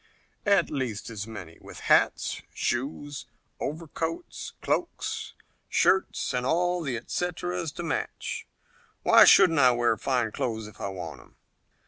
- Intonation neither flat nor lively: No, wide, 7.3 semitones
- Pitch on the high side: No, medium, 140 Hz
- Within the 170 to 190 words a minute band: No, slow, 135 wpm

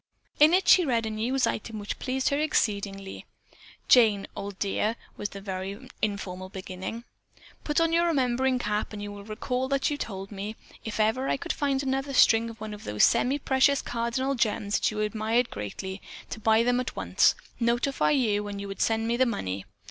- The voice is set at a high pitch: Yes, high, 225 Hz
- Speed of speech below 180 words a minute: No, average, 195 wpm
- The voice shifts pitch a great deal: No, average, 4.4 semitones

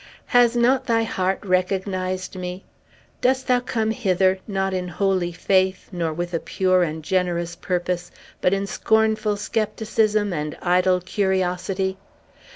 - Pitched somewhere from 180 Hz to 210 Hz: Yes, high, 190 Hz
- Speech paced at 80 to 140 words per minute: Yes, slow, 135 wpm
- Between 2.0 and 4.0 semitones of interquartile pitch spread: Yes, average, 2.9 semitones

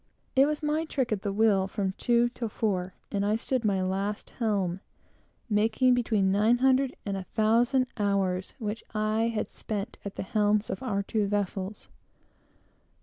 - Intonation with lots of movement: No, average, 3.1 semitones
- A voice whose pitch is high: Yes, high, 215 Hz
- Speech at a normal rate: Yes, average, 165 wpm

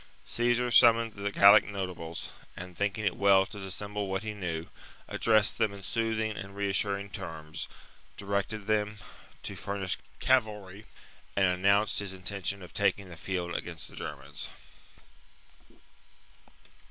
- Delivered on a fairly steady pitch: Yes, narrow, 2.0 semitones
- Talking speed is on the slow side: Yes, slow, 130 wpm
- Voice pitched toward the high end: No, low, 100 Hz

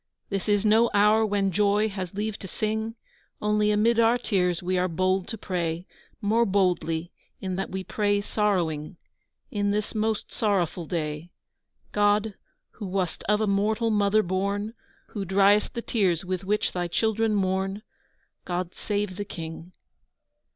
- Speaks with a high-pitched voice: Yes, high, 200 Hz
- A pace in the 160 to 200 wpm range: No, average, 150 wpm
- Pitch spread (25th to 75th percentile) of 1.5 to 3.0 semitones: Yes, narrow, 2.5 semitones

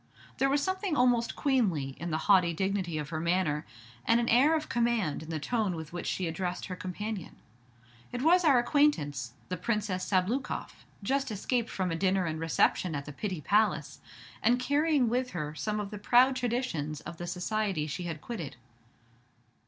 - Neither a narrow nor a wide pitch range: No, wide, 6.8 semitones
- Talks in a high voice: Yes, high, 195 Hz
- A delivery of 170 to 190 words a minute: Yes, average, 180 wpm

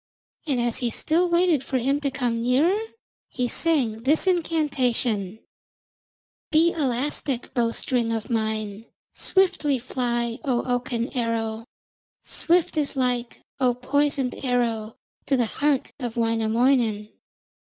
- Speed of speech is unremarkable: No, slow, 120 wpm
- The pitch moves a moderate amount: Yes, average, 3.9 semitones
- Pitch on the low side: No, very high, 250 Hz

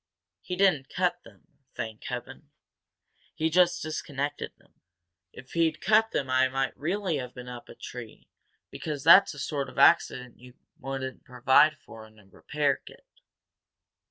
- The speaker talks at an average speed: Yes, average, 155 wpm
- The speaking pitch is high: No, medium, 140 Hz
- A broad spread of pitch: No, average, 4.7 semitones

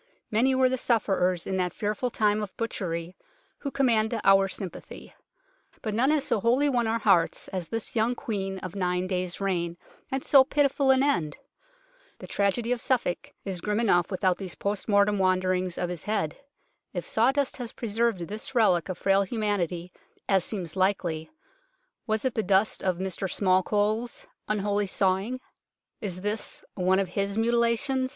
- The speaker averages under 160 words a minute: No, average, 170 wpm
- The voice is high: Yes, high, 205 Hz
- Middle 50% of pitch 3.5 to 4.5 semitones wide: Yes, average, 3.9 semitones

